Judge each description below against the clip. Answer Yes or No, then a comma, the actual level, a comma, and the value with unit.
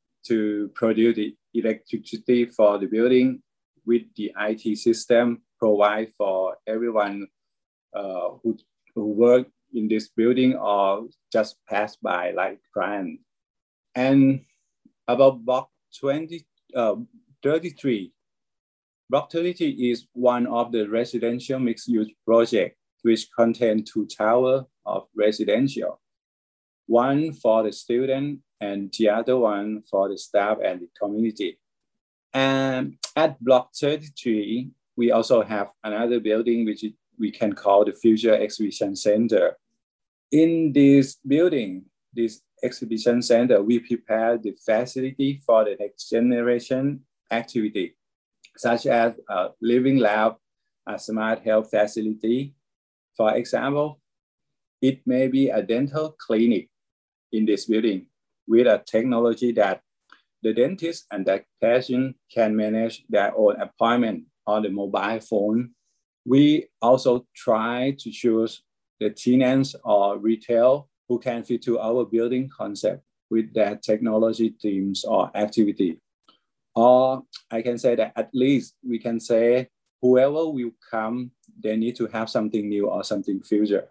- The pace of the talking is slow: Yes, slow, 130 wpm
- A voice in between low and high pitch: No, low, 115 Hz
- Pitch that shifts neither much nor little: Yes, average, 3.1 semitones